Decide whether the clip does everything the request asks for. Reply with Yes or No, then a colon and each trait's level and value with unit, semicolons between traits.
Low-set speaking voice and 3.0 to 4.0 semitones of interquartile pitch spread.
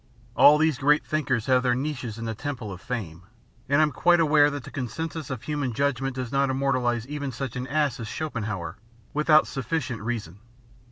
Yes: low, 130 Hz; average, 3.6 semitones